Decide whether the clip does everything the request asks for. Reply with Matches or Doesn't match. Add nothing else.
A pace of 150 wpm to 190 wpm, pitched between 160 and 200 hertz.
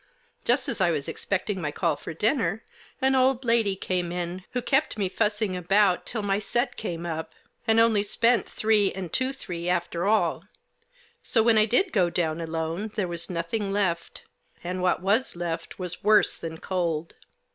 Matches